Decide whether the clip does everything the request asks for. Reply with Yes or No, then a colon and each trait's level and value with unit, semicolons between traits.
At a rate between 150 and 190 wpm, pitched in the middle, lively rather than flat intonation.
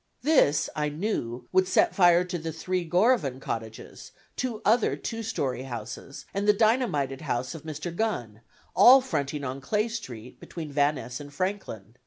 Yes: average, 165 wpm; medium, 160 Hz; wide, 7.8 semitones